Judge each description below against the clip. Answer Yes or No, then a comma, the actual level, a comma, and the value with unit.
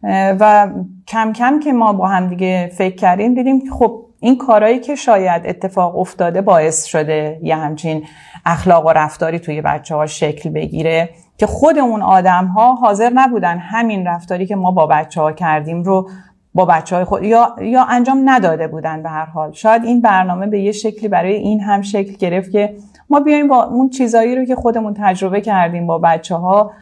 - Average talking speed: No, fast, 185 wpm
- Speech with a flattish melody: No, average, 5.1 semitones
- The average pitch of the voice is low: No, high, 190 Hz